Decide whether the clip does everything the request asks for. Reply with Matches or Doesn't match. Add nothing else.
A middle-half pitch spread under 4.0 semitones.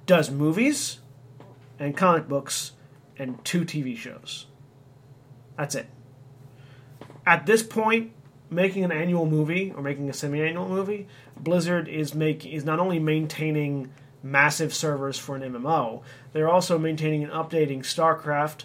Matches